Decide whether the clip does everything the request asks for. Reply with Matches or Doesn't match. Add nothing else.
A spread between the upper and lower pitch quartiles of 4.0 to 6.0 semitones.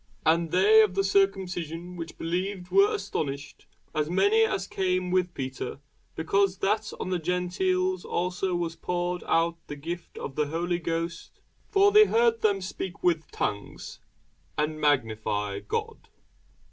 Doesn't match